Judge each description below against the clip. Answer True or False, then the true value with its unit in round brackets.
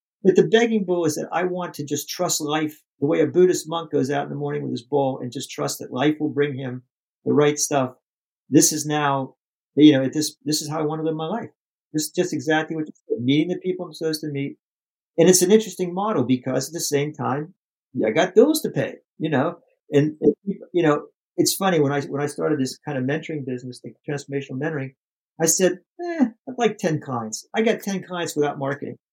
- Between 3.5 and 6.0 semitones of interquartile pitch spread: True (4.0 semitones)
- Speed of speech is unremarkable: False (235 wpm)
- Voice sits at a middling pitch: True (155 Hz)